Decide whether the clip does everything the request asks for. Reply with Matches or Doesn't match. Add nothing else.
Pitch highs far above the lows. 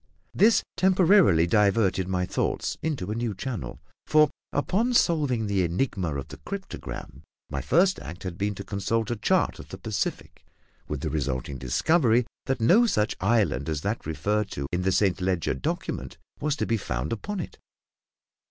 Matches